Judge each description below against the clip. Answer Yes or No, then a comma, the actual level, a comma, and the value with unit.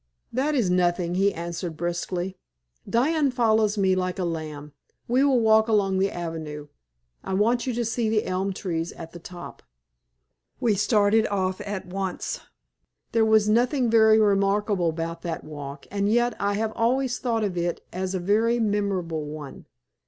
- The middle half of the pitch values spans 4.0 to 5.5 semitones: Yes, average, 4.3 semitones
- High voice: Yes, high, 200 Hz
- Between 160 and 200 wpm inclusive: Yes, average, 165 wpm